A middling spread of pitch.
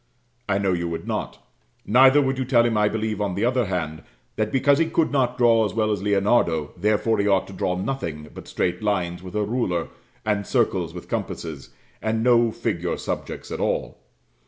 Yes: average, 4.7 semitones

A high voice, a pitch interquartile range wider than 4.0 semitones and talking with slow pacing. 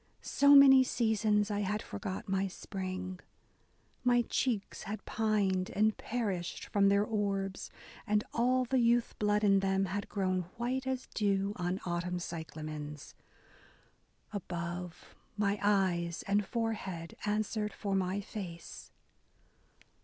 No: high, 200 Hz; average, 2.7 semitones; slow, 125 wpm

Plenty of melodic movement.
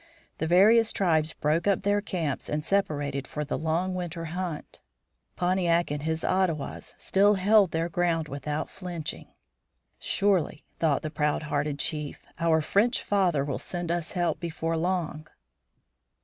No: average, 3.3 semitones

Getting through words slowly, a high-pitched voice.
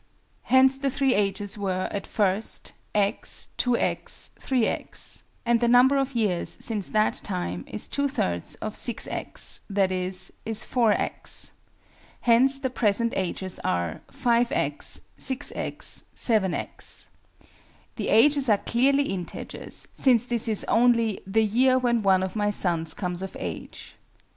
Yes: slow, 130 wpm; high, 220 Hz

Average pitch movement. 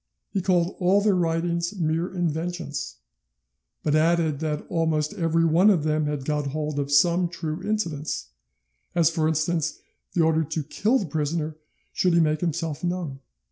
No: narrow, 2.3 semitones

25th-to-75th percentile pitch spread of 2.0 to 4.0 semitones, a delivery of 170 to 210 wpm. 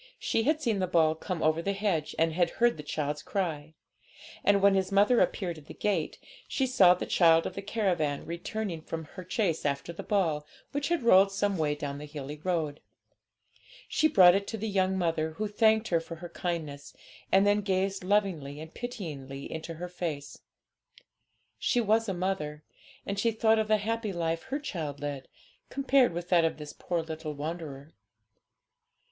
No: average, 4.6 semitones; average, 185 wpm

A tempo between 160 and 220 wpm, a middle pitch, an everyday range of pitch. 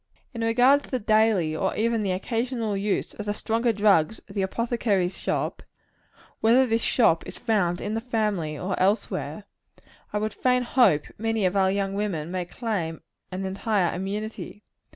No: average, 170 wpm; high, 210 Hz; average, 3.1 semitones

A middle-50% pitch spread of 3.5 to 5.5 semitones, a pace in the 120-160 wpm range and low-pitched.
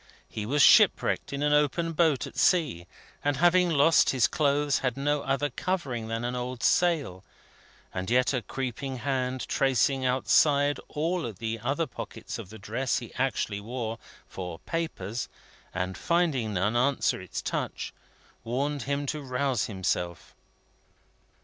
Yes: average, 4.2 semitones; average, 150 wpm; low, 130 Hz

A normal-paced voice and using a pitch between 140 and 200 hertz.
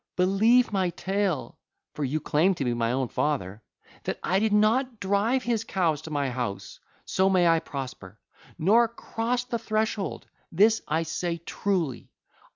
Yes: average, 150 wpm; medium, 185 Hz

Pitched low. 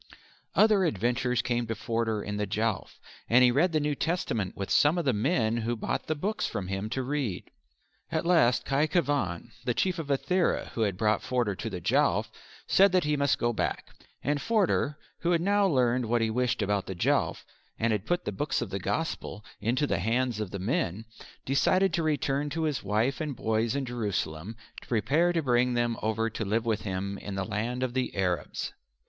Yes: low, 120 Hz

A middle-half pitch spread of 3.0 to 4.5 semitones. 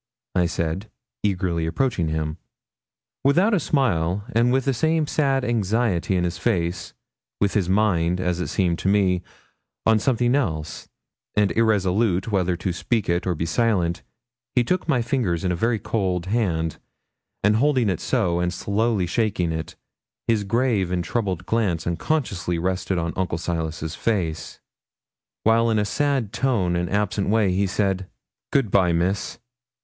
No: average, 4.9 semitones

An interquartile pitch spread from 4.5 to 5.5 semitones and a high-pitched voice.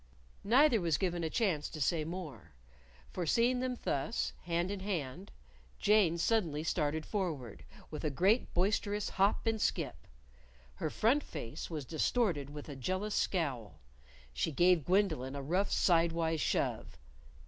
No: average, 5.2 semitones; medium, 170 Hz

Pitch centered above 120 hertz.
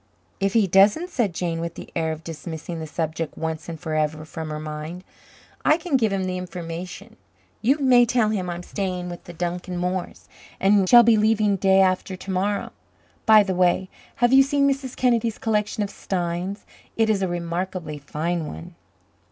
Yes: medium, 185 Hz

